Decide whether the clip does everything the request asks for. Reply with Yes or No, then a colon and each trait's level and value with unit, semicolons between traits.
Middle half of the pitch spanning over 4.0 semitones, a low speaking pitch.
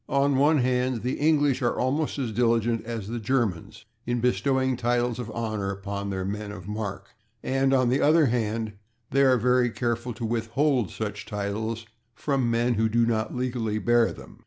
No: average, 2.9 semitones; low, 120 Hz